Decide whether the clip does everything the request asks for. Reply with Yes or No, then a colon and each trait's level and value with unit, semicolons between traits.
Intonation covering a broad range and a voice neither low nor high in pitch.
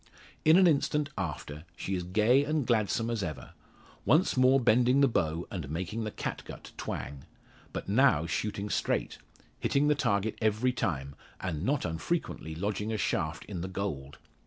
No: wide, 7.1 semitones; low, 105 Hz